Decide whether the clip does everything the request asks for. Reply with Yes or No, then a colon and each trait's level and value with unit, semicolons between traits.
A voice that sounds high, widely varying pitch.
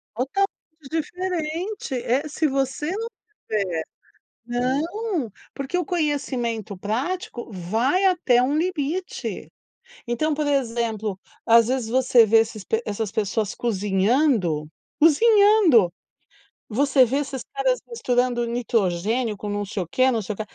Yes: very high, 255 Hz; wide, 6.0 semitones